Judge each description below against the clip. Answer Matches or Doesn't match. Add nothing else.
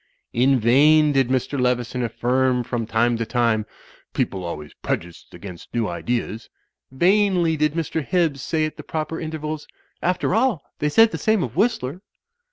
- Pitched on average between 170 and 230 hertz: Doesn't match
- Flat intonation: Doesn't match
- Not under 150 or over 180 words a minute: Matches